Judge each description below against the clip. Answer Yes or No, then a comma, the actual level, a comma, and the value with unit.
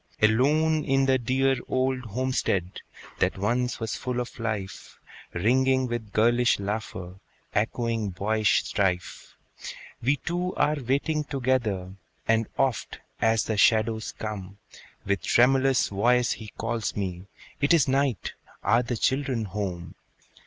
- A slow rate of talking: Yes, slow, 125 wpm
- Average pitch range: Yes, average, 4.0 semitones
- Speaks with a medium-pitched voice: No, low, 115 Hz